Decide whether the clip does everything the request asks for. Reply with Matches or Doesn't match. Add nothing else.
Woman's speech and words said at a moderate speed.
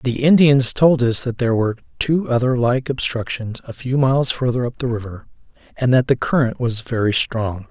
Doesn't match